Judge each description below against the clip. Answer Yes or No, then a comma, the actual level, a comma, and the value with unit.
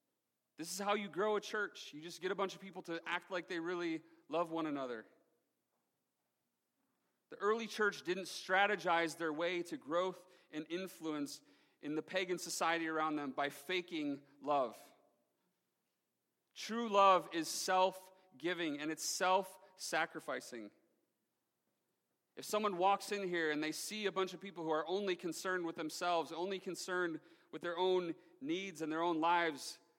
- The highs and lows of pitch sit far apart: No, average, 3.2 semitones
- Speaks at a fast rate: No, average, 160 wpm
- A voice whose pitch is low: No, medium, 180 Hz